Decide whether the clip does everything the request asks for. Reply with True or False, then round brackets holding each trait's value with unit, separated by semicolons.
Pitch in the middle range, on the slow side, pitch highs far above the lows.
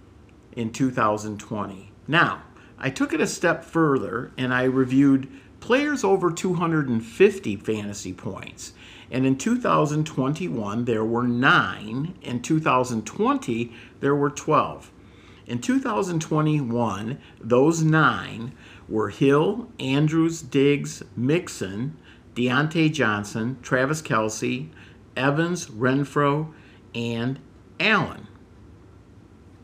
False (125 Hz; 90 wpm; 5.9 semitones)